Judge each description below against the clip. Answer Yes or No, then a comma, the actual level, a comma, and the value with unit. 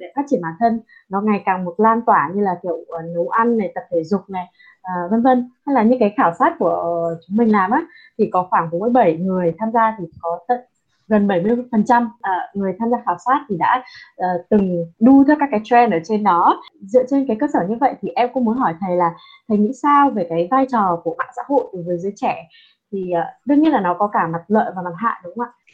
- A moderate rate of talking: No, fast, 255 wpm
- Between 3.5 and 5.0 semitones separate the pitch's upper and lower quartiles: No, wide, 5.5 semitones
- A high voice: Yes, high, 215 Hz